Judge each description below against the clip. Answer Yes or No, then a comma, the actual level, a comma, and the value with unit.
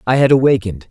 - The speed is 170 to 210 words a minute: Yes, average, 200 wpm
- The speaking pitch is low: Yes, low, 120 Hz